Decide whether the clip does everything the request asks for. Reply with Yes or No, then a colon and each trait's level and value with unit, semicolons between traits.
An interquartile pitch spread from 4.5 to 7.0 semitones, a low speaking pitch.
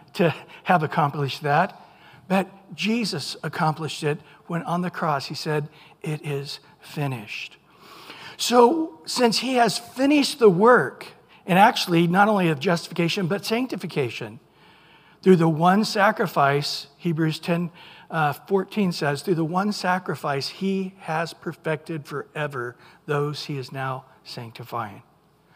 No: average, 4.8 semitones; medium, 170 Hz